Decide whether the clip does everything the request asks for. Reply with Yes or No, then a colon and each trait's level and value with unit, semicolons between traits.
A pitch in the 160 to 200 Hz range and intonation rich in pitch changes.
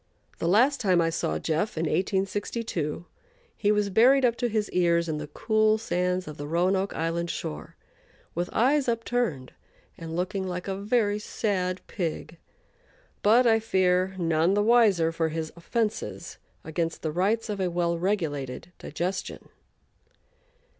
No: medium, 185 Hz; average, 4.3 semitones